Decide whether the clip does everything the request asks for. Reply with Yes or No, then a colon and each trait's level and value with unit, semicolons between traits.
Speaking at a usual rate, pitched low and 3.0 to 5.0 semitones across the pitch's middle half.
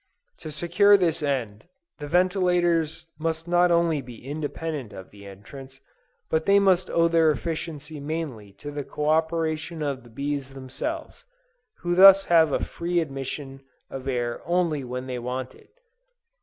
No: average, 155 wpm; medium, 155 Hz; average, 4.2 semitones